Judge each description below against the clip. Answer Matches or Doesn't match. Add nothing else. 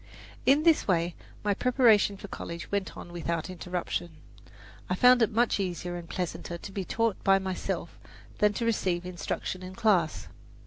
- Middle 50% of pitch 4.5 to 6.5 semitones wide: Doesn't match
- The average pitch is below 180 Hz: Doesn't match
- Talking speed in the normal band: Matches